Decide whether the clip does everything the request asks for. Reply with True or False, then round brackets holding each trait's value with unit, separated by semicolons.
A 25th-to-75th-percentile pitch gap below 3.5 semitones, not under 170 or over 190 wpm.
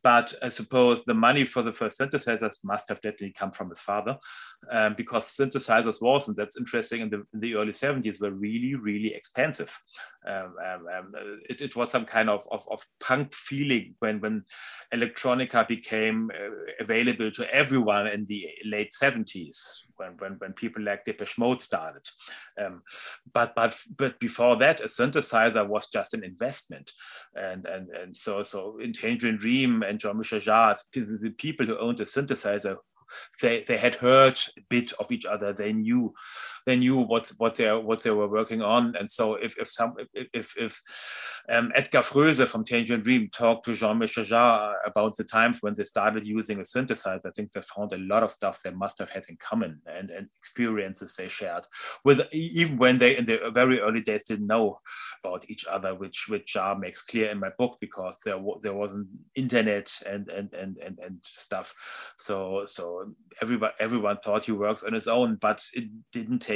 True (3.1 semitones; 185 wpm)